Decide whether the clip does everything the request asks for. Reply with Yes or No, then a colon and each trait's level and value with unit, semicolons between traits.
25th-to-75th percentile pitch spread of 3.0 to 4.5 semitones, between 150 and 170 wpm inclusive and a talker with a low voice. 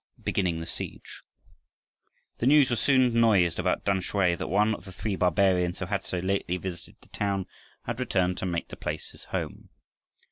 No: average, 3.3 semitones; average, 180 wpm; very low, 95 Hz